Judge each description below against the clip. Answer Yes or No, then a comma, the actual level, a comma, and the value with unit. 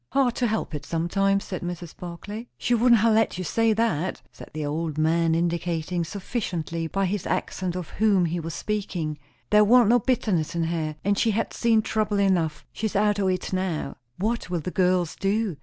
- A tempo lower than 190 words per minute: No, average, 195 wpm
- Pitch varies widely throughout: No, average, 4.1 semitones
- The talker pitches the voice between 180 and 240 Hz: Yes, medium, 185 Hz